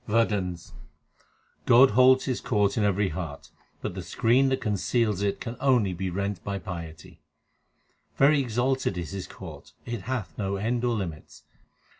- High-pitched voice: No, low, 105 Hz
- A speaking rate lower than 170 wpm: Yes, average, 155 wpm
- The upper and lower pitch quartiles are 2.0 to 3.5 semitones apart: No, average, 4.6 semitones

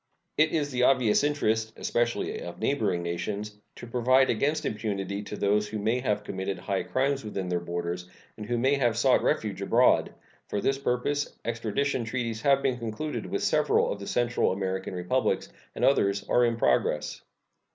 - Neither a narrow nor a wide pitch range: Yes, average, 4.3 semitones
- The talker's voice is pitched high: No, low, 110 Hz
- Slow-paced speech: No, average, 170 wpm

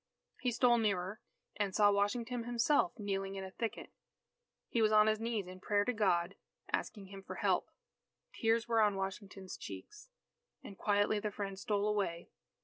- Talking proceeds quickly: No, average, 165 wpm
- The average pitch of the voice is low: No, high, 205 Hz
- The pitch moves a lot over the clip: No, narrow, 2.6 semitones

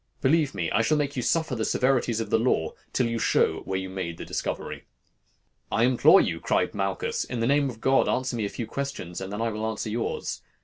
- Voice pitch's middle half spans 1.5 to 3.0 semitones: No, average, 4.4 semitones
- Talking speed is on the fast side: Yes, fast, 230 wpm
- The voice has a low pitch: Yes, low, 115 Hz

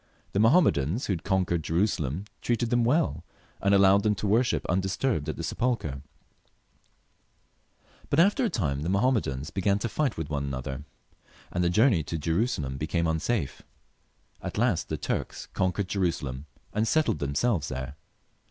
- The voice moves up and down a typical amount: No, wide, 7.1 semitones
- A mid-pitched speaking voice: No, very low, 95 Hz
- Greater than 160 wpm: No, average, 155 wpm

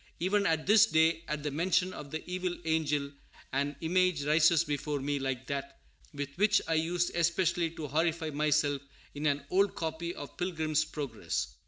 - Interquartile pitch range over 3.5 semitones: No, average, 3.1 semitones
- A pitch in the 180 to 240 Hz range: No, medium, 160 Hz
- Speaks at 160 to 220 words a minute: Yes, average, 170 wpm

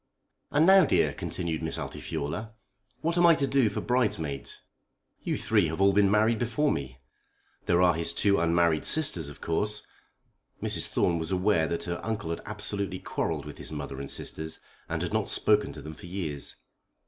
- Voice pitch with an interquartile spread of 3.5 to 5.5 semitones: Yes, average, 5.2 semitones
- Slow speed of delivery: No, average, 185 wpm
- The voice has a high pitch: No, very low, 90 Hz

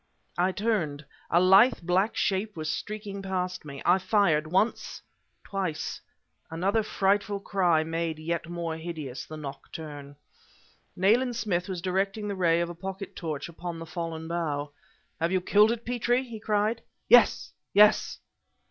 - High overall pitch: No, medium, 180 Hz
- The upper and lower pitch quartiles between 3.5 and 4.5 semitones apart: Yes, average, 3.9 semitones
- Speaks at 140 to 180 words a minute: Yes, average, 150 wpm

